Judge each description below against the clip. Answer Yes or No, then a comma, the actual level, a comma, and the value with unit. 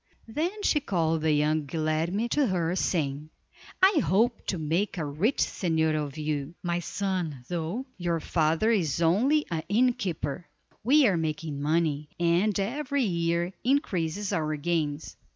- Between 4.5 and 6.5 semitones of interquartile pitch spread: Yes, average, 5.0 semitones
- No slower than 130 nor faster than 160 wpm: Yes, average, 145 wpm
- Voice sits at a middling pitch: Yes, medium, 170 Hz